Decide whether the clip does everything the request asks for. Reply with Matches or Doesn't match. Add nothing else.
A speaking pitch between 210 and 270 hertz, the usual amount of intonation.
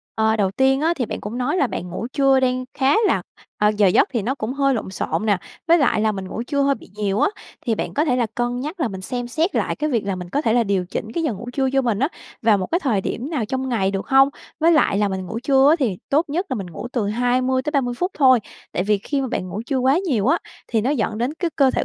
Matches